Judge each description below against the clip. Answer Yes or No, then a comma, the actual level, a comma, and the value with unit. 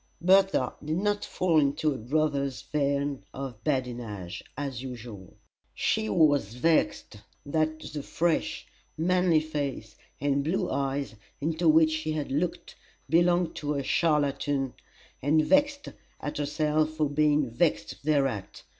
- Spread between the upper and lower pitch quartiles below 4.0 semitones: Yes, average, 2.8 semitones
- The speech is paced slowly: Yes, slow, 130 wpm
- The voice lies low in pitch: No, medium, 145 Hz